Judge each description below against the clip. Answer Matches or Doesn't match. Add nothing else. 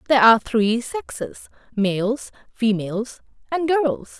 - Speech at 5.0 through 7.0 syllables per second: Doesn't match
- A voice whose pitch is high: Matches